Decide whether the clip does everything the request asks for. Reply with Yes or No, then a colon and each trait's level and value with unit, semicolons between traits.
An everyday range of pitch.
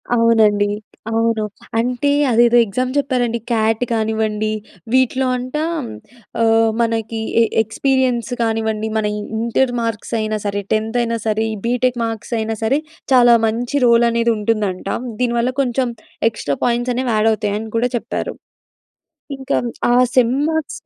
No: narrow, 2.0 semitones